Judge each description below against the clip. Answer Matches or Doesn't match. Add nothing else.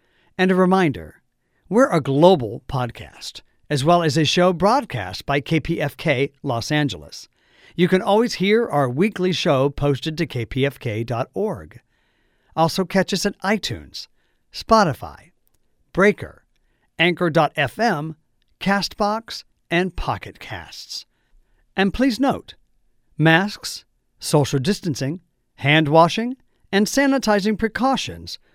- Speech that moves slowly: Matches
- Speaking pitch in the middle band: Matches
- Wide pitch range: Matches